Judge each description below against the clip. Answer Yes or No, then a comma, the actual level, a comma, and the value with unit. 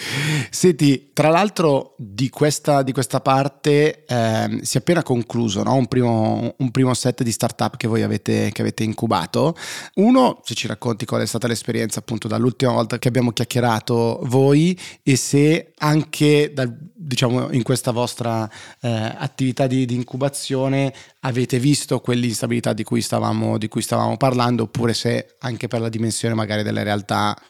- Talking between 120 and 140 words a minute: No, average, 160 wpm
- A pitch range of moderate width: Yes, average, 3.1 semitones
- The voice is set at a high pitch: No, low, 125 Hz